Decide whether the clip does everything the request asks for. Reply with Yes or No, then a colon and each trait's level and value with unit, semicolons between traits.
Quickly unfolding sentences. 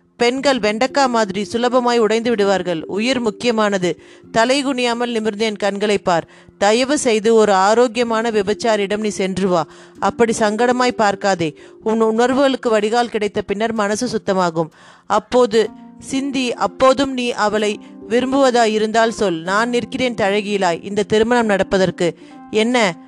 No: average, 120 wpm